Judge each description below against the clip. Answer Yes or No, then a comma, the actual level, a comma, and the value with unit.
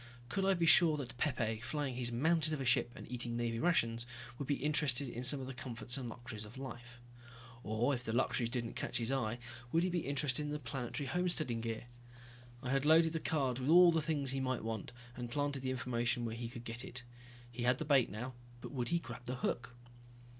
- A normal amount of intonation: Yes, average, 3.6 semitones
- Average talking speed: No, fast, 225 wpm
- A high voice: No, low, 130 Hz